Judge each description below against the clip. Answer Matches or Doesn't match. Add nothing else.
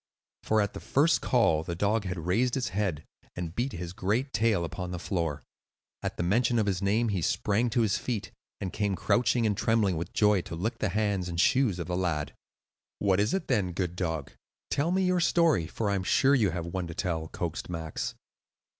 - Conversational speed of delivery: Doesn't match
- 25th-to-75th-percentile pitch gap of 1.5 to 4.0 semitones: Doesn't match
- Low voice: Matches